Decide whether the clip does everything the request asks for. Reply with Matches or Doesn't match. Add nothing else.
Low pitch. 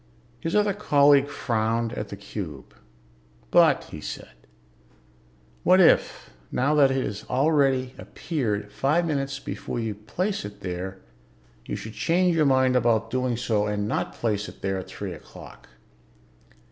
Matches